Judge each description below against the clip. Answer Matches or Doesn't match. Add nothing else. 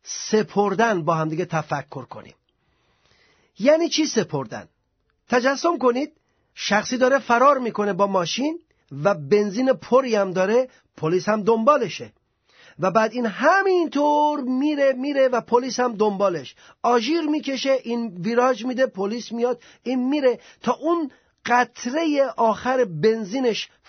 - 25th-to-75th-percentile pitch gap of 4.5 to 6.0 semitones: Matches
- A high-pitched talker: Matches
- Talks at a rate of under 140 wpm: Matches